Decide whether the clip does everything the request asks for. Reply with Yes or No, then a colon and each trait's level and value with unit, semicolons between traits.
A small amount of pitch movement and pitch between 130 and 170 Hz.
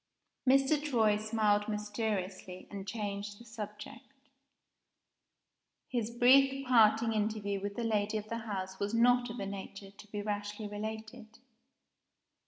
No: narrow, 2.1 semitones; high, 215 Hz